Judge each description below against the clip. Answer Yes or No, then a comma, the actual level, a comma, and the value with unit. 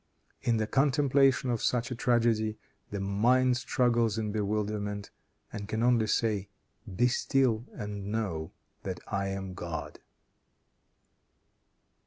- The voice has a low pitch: Yes, low, 110 Hz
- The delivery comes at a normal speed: No, slow, 120 wpm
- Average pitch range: Yes, average, 3.3 semitones